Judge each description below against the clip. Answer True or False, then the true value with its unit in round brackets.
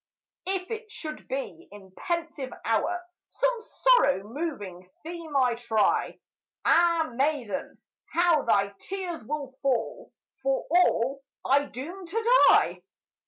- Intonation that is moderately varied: False (5.9 semitones)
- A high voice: True (300 Hz)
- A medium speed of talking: False (120 wpm)